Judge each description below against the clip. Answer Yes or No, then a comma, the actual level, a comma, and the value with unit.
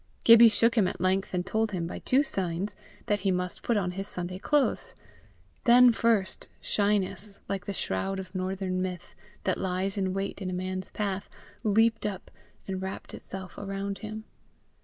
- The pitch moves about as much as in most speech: No, narrow, 2.3 semitones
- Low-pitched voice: No, high, 195 Hz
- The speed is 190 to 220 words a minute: No, average, 175 wpm